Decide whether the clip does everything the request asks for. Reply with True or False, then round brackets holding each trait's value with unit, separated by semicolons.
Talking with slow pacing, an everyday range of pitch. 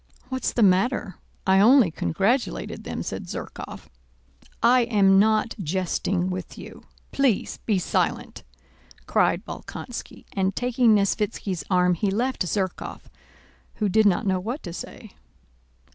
True (130 wpm; 3.8 semitones)